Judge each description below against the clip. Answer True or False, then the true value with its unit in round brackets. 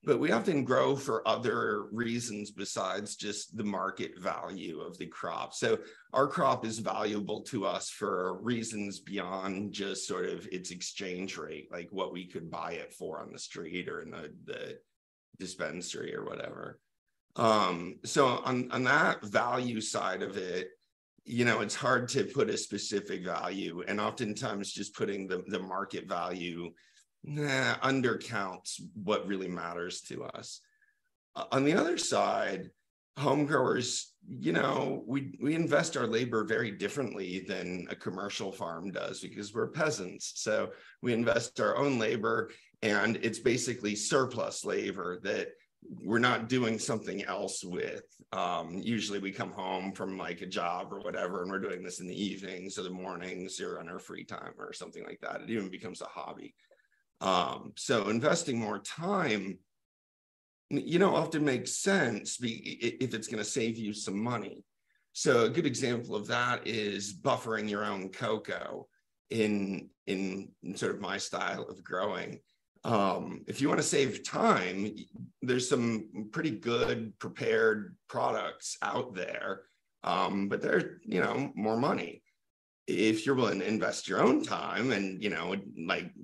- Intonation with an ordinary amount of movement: True (4.1 semitones)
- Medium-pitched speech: False (105 Hz)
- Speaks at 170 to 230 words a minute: False (160 wpm)